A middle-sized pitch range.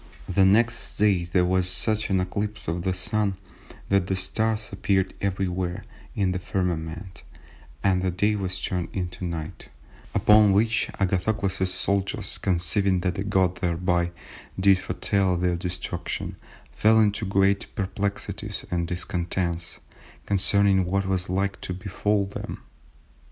No: narrow, 1.8 semitones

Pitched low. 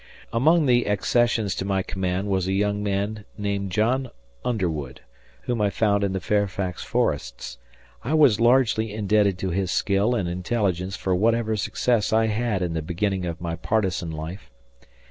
Yes: low, 100 Hz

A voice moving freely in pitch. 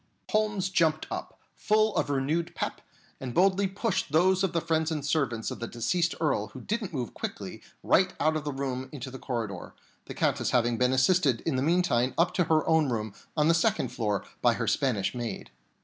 Yes: wide, 5.9 semitones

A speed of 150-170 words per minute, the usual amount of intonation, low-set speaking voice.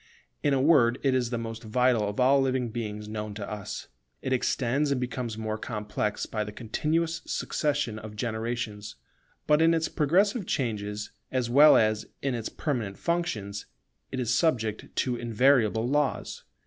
Yes: average, 160 wpm; average, 4.3 semitones; low, 120 Hz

